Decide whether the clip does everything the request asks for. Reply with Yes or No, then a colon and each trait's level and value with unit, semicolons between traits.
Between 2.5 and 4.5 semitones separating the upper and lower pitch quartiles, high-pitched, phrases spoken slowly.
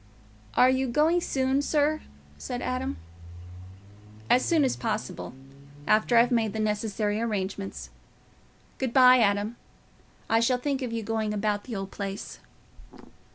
Yes: average, 3.8 semitones; high, 225 Hz; slow, 130 wpm